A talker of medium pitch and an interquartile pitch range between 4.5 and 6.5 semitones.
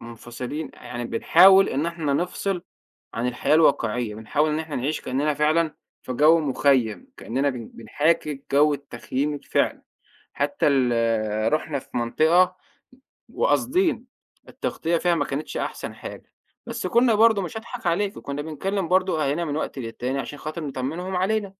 Yes: medium, 150 Hz; average, 5.2 semitones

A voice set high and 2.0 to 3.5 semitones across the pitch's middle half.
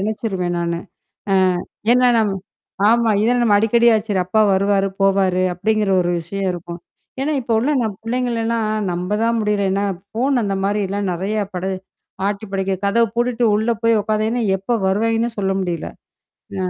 Yes: high, 210 Hz; average, 3.0 semitones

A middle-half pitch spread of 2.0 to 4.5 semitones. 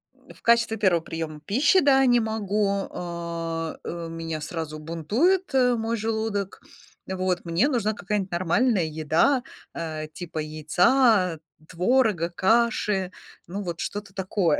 No: average, 5.2 semitones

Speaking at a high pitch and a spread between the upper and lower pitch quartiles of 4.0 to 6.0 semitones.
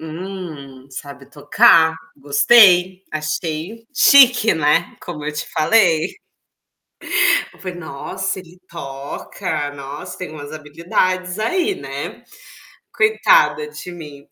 No: medium, 165 Hz; average, 4.5 semitones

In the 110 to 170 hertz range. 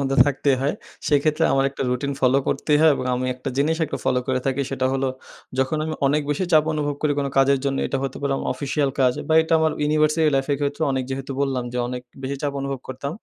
Yes: medium, 140 Hz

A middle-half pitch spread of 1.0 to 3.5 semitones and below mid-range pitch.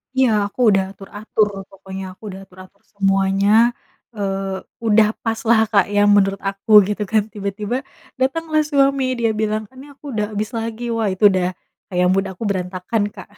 No: narrow, 2.6 semitones; high, 205 Hz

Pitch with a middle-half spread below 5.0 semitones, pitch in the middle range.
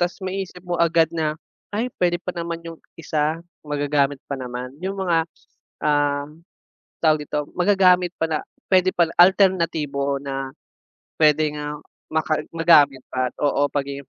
Yes: average, 3.5 semitones; medium, 155 Hz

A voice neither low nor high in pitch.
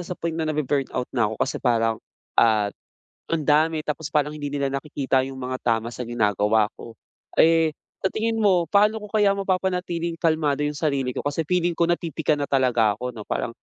Yes: medium, 145 Hz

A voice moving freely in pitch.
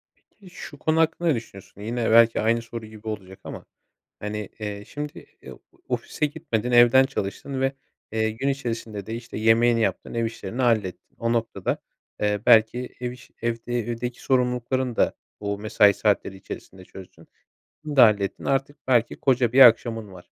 No: average, 2.9 semitones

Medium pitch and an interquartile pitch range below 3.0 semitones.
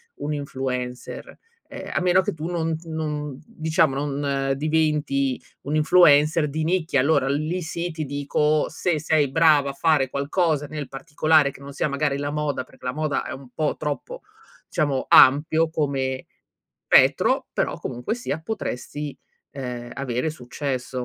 Yes: medium, 150 Hz; narrow, 2.4 semitones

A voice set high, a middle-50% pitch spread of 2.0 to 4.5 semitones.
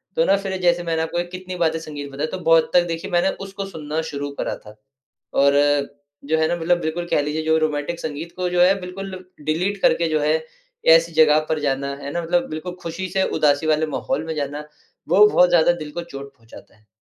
No: medium, 160 Hz; average, 2.8 semitones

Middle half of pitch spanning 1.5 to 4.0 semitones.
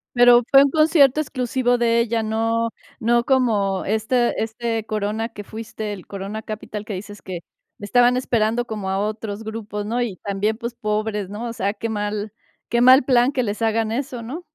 Yes: narrow, 2.4 semitones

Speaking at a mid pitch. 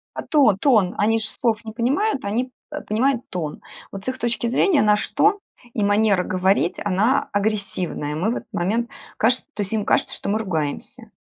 No: high, 215 Hz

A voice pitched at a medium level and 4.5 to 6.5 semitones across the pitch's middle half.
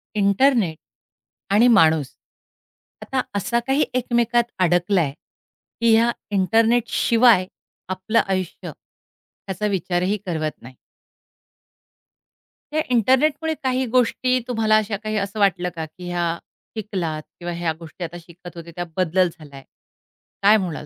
No: high, 195 Hz; average, 5.1 semitones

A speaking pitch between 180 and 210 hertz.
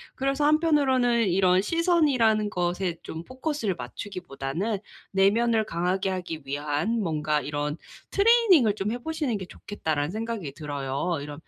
Yes: high, 195 Hz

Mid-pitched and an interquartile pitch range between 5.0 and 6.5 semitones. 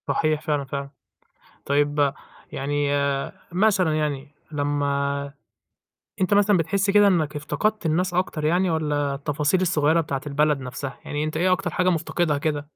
No: medium, 150 Hz; average, 3.8 semitones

